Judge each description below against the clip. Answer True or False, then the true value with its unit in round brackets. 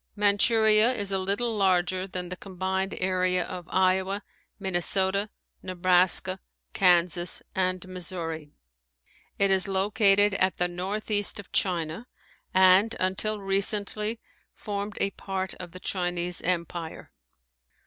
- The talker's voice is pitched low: False (190 Hz)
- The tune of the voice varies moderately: False (1.8 semitones)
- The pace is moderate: False (115 wpm)